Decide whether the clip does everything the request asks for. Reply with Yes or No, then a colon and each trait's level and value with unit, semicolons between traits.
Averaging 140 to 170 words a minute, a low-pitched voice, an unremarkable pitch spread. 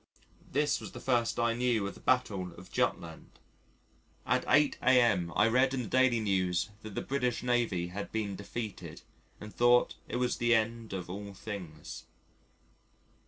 Yes: average, 165 wpm; low, 115 Hz; average, 3.9 semitones